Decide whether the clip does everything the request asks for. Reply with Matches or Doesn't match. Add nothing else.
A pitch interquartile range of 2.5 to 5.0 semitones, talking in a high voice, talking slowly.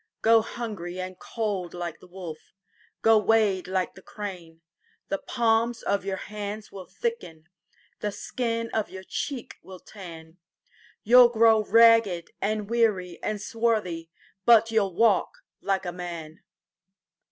Matches